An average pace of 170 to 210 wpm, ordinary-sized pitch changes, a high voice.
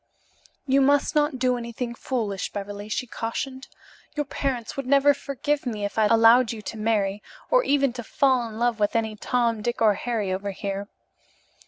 Yes: average, 180 wpm; average, 3.8 semitones; high, 235 Hz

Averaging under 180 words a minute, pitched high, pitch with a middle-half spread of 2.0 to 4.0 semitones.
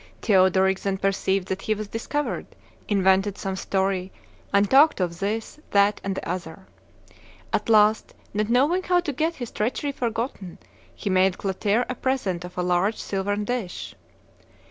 Yes: average, 155 wpm; high, 200 Hz; average, 3.5 semitones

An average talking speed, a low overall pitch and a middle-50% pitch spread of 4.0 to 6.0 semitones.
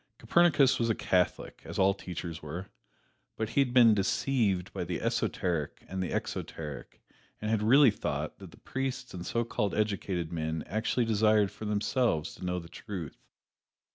Yes: average, 170 wpm; low, 105 Hz; average, 4.7 semitones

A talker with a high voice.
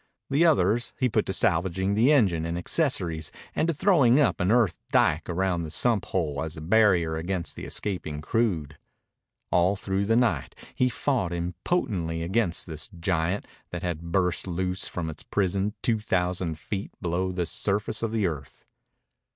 No: very low, 95 Hz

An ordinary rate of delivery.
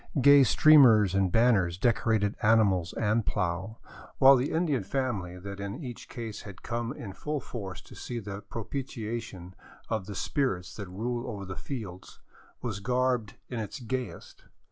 Yes: average, 160 wpm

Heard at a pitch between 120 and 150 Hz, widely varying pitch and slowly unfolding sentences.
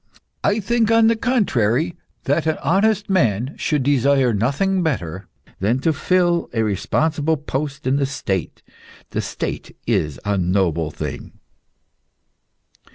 Yes: medium, 140 Hz; wide, 8.8 semitones; slow, 130 wpm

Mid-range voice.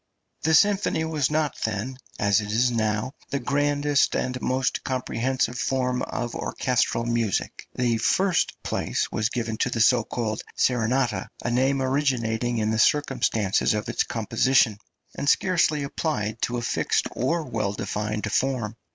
No: low, 125 Hz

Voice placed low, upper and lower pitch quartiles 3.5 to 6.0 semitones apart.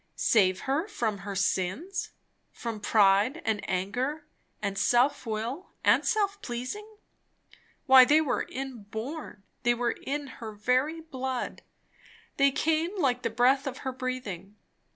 No: very high, 255 Hz; average, 5.2 semitones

